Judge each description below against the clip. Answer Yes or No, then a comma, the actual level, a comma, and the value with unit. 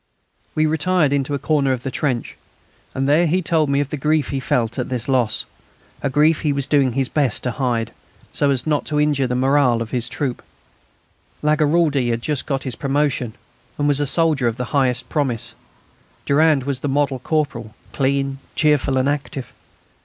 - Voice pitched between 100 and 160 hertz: Yes, medium, 140 Hz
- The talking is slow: No, average, 190 wpm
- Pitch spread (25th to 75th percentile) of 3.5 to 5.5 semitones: No, average, 2.7 semitones